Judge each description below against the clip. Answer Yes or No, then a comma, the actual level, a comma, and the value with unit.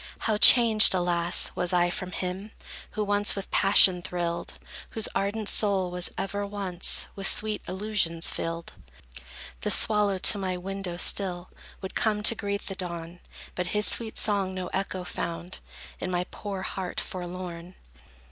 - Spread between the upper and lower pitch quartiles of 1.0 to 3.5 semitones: Yes, narrow, 2.4 semitones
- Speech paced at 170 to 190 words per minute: No, average, 150 wpm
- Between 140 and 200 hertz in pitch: Yes, high, 190 Hz